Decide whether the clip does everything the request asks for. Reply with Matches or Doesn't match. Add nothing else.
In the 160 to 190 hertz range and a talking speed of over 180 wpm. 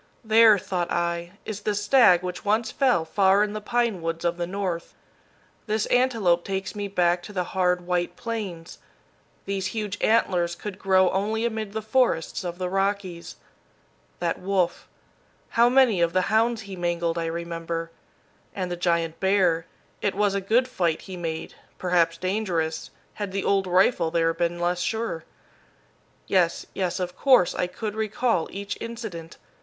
Doesn't match